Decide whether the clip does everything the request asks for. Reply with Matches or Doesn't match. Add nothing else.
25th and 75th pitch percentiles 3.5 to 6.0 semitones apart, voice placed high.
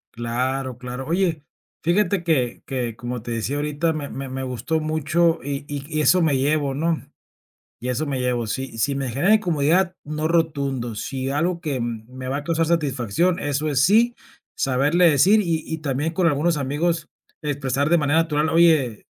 Doesn't match